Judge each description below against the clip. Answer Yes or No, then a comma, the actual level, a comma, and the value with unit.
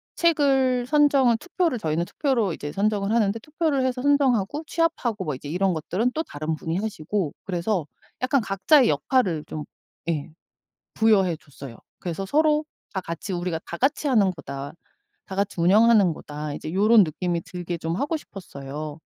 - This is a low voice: No, high, 195 Hz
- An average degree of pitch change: No, wide, 7.6 semitones